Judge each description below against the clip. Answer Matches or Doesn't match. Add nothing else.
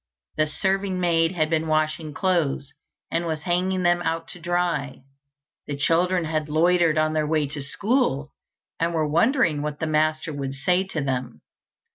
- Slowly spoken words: Doesn't match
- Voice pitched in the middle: Matches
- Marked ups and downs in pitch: Doesn't match